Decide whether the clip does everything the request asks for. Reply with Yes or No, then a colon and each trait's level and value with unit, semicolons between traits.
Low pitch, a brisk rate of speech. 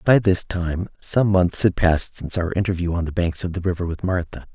Yes: very low, 90 Hz; fast, 235 wpm